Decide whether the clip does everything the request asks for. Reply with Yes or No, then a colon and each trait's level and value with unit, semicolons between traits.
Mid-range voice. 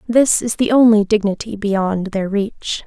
No: high, 210 Hz